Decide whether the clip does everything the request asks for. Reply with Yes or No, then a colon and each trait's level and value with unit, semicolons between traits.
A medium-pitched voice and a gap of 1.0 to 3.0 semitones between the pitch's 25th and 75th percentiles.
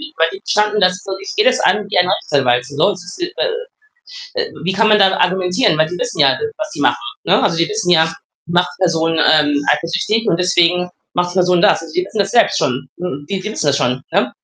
No: medium, 180 Hz; average, 4.0 semitones